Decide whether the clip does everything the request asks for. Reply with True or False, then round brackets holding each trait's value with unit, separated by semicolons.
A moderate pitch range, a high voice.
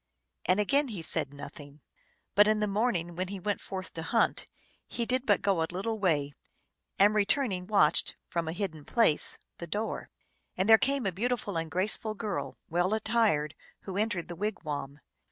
True (4.4 semitones; 195 Hz)